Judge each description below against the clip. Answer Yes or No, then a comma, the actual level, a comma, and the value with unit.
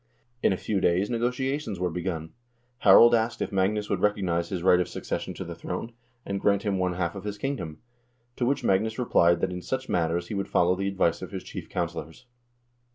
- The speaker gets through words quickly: Yes, fast, 210 wpm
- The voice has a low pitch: Yes, very low, 95 Hz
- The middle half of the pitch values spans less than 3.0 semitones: No, average, 4.0 semitones